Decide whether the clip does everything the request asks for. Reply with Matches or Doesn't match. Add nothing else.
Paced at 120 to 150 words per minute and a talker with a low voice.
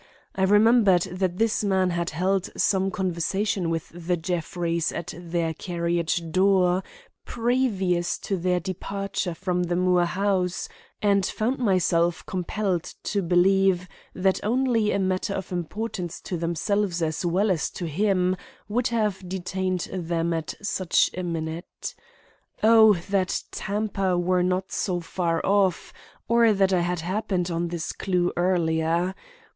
Doesn't match